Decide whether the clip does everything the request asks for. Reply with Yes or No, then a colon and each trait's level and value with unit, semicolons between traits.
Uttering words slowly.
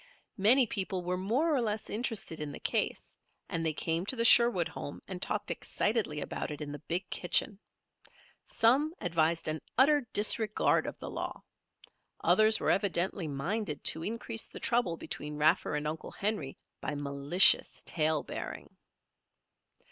No: average, 155 wpm